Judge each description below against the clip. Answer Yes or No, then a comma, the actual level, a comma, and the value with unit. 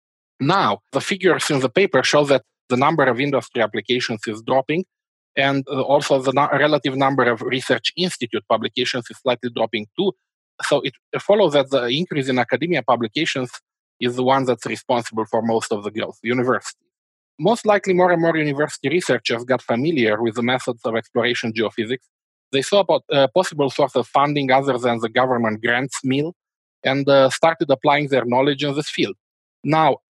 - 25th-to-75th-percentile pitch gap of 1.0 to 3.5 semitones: Yes, average, 3.1 semitones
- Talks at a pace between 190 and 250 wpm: No, average, 175 wpm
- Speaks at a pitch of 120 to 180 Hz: Yes, low, 135 Hz